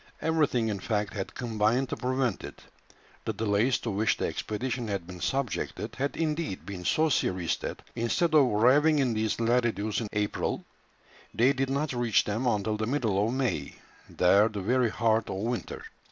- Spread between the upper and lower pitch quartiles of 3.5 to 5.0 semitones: Yes, average, 4.0 semitones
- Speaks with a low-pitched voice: Yes, low, 115 Hz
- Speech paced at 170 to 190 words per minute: Yes, average, 175 wpm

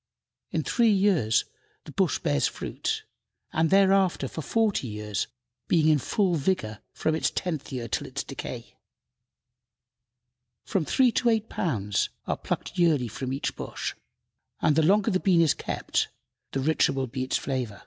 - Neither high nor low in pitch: Yes, medium, 155 Hz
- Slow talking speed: No, average, 160 wpm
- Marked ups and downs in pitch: Yes, wide, 6.8 semitones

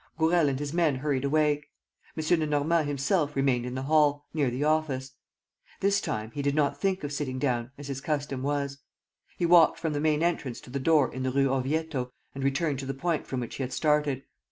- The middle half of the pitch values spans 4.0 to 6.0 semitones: No, narrow, 2.6 semitones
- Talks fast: Yes, fast, 215 wpm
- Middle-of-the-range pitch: Yes, medium, 145 Hz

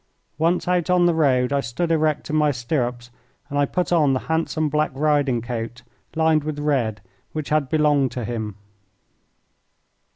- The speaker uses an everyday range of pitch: Yes, average, 4.0 semitones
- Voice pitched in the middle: Yes, medium, 145 Hz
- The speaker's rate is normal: Yes, average, 165 wpm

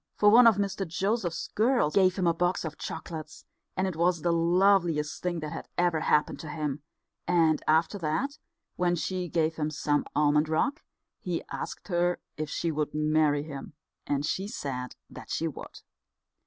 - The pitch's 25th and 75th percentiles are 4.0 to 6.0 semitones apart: No, average, 3.3 semitones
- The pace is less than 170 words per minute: No, average, 175 wpm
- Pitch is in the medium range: Yes, medium, 165 Hz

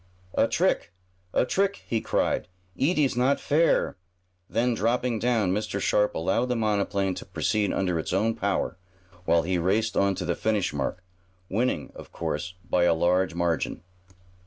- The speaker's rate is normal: Yes, average, 160 wpm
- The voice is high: No, low, 100 Hz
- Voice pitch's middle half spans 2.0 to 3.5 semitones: No, average, 4.4 semitones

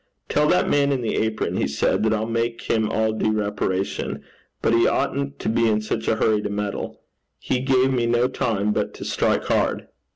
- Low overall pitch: Yes, low, 110 Hz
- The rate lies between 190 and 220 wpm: Yes, fast, 205 wpm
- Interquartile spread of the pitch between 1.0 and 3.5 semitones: Yes, average, 2.8 semitones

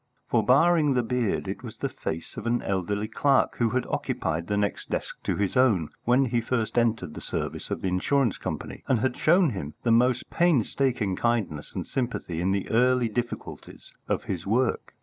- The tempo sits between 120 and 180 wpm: No, average, 190 wpm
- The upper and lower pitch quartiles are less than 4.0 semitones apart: No, average, 4.3 semitones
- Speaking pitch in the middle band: No, low, 115 Hz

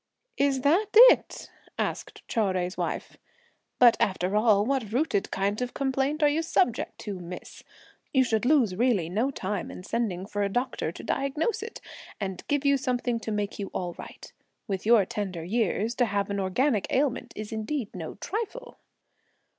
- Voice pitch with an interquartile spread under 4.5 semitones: No, wide, 5.4 semitones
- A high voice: Yes, high, 225 Hz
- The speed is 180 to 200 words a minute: No, average, 170 wpm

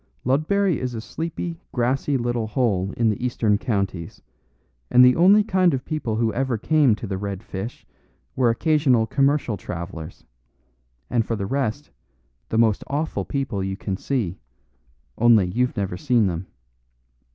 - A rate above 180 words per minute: No, average, 150 wpm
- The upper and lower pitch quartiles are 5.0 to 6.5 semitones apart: Yes, average, 5.3 semitones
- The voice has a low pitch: Yes, low, 120 Hz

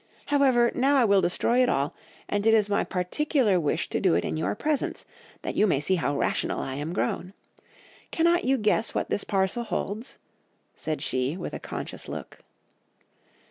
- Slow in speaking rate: No, average, 180 wpm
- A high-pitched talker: Yes, high, 205 Hz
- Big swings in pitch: Yes, wide, 6.9 semitones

